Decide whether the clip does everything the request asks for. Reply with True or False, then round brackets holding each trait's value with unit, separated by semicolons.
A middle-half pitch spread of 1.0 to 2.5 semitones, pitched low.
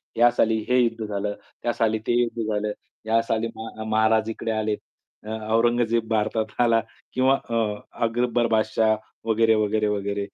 True (1.3 semitones; 110 Hz)